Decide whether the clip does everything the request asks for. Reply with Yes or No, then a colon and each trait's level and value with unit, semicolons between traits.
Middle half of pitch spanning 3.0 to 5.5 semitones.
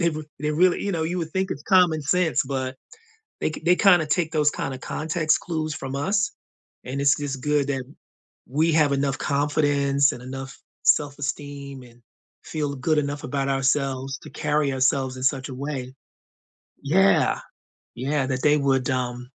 No: narrow, 2.6 semitones